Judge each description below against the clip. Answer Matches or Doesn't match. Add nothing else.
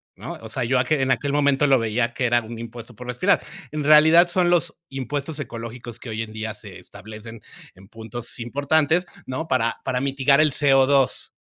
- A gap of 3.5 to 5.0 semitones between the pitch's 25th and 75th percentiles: Matches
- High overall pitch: Doesn't match